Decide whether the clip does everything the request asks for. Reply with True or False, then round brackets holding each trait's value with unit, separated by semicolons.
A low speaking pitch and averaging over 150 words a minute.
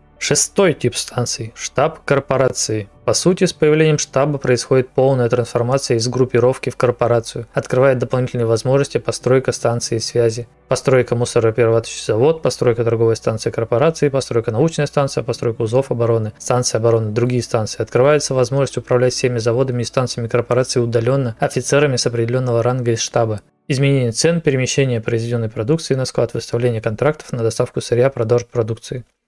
False (125 Hz; 140 wpm)